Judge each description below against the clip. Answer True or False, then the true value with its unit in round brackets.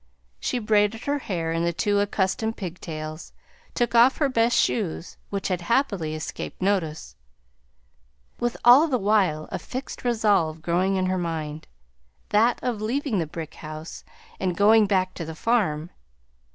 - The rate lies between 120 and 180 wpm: True (155 wpm)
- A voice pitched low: False (195 Hz)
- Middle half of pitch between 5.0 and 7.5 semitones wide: True (5.6 semitones)